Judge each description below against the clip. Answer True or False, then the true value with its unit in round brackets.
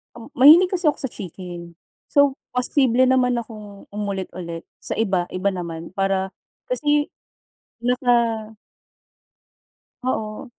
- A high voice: True (220 Hz)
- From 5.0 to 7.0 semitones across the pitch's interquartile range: True (5.3 semitones)